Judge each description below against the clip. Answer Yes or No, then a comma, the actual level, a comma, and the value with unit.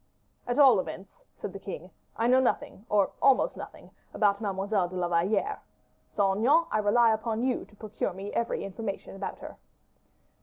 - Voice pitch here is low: No, high, 215 Hz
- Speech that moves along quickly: No, average, 175 wpm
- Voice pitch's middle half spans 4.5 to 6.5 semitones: No, average, 3.7 semitones